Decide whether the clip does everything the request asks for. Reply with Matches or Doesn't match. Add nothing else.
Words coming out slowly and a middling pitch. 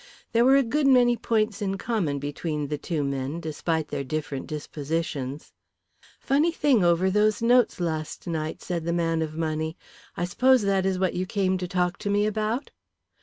Doesn't match